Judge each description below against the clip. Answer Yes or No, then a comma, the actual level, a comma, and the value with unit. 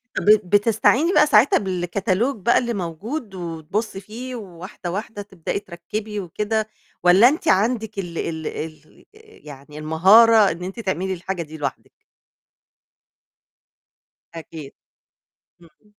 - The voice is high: Yes, high, 195 Hz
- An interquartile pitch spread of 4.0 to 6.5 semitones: Yes, average, 4.4 semitones